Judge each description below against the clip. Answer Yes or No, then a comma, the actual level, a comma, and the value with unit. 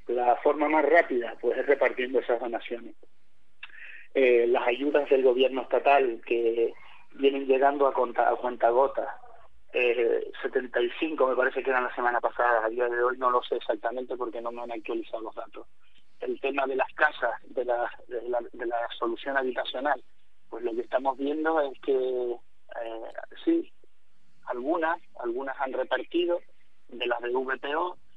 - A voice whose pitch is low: Yes, low, 130 Hz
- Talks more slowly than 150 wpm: No, average, 165 wpm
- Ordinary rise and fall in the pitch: Yes, average, 4.3 semitones